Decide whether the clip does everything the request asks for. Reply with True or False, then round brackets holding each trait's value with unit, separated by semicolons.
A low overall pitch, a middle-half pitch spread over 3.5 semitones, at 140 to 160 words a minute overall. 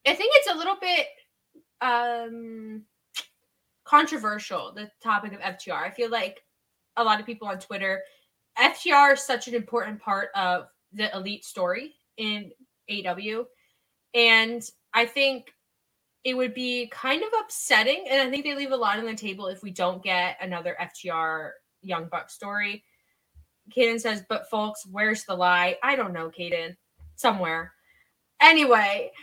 False (215 Hz; 4.9 semitones; 150 wpm)